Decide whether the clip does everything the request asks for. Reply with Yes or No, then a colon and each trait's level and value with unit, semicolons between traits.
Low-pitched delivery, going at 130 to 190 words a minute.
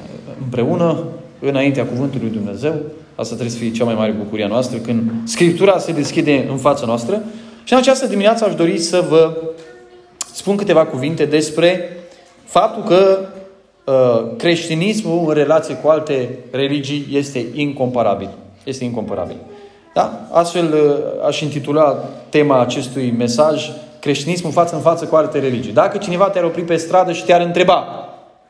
No: medium, 155 Hz; average, 150 wpm